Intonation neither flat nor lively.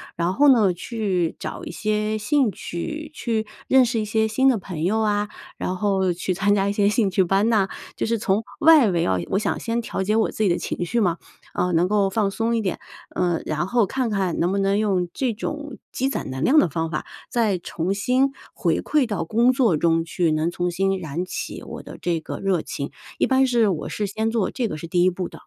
Yes: average, 4.3 semitones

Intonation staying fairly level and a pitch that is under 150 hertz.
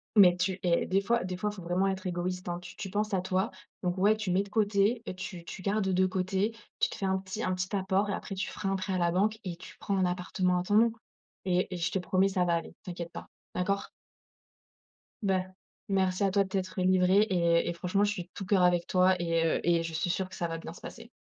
No: narrow, 1.7 semitones; medium, 185 Hz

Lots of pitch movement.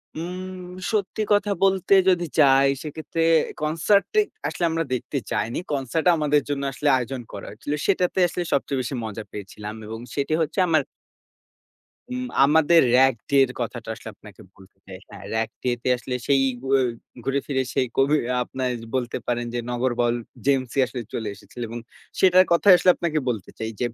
Yes: wide, 5.8 semitones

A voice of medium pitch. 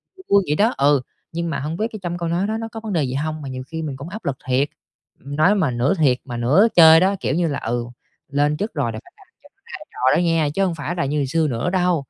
Yes: medium, 155 Hz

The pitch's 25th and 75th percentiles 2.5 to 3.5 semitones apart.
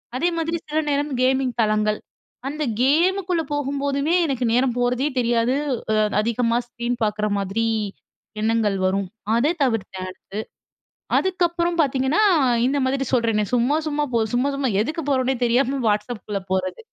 No: average, 4.2 semitones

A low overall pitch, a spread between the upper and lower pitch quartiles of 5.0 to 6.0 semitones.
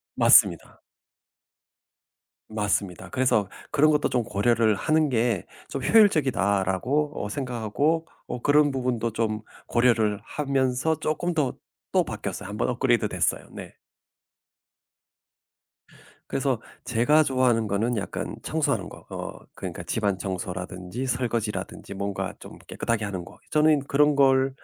Yes: low, 120 Hz; average, 5.3 semitones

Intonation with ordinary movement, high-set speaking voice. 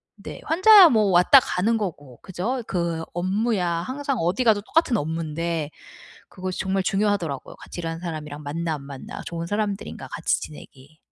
No: average, 4.7 semitones; medium, 180 Hz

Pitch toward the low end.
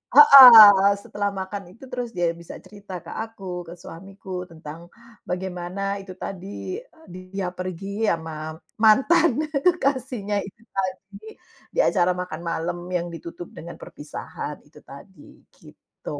No: high, 195 Hz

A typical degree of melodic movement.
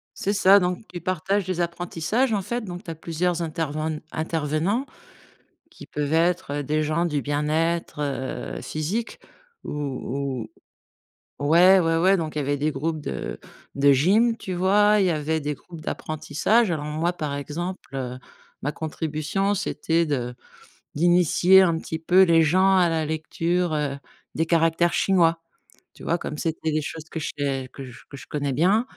Yes: average, 3.3 semitones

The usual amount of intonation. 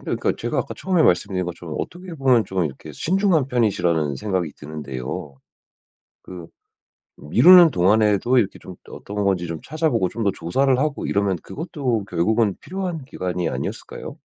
No: wide, 7.8 semitones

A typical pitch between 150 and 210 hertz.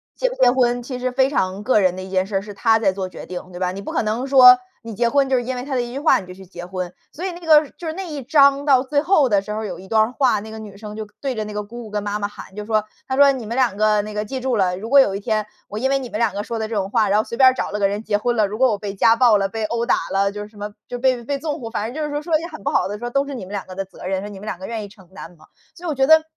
No: high, 220 Hz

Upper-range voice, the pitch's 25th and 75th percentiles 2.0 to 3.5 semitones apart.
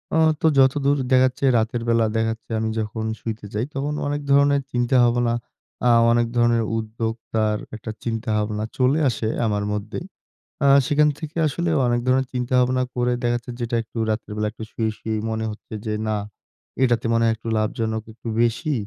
No: low, 120 Hz; narrow, 2.6 semitones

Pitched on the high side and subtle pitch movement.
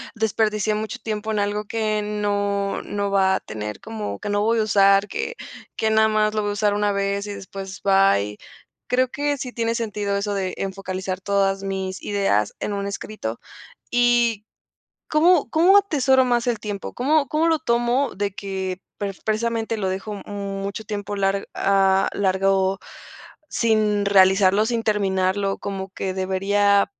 Yes: high, 205 Hz; narrow, 2.1 semitones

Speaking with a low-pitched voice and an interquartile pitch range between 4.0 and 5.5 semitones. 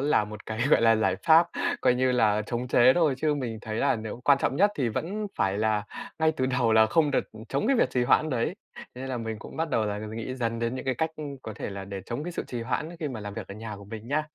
Yes: low, 120 Hz; average, 4.5 semitones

